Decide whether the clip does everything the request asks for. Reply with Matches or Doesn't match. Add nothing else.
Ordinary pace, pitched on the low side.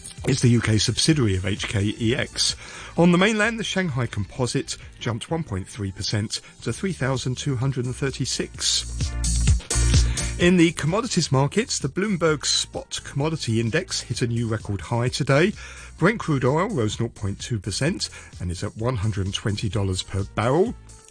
Doesn't match